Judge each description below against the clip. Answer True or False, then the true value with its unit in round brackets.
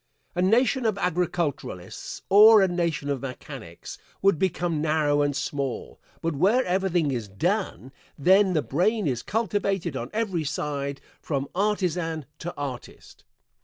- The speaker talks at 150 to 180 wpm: False (135 wpm)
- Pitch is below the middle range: False (170 Hz)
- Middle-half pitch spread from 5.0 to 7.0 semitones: True (5.4 semitones)